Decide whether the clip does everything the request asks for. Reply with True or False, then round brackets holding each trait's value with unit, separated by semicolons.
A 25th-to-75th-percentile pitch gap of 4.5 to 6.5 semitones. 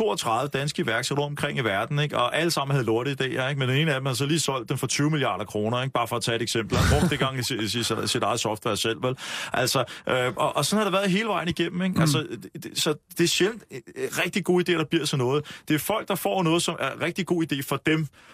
True (5.5 semitones)